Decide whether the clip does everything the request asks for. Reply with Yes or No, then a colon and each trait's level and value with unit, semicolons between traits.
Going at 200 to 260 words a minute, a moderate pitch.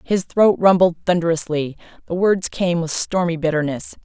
No: average, 150 wpm; medium, 170 Hz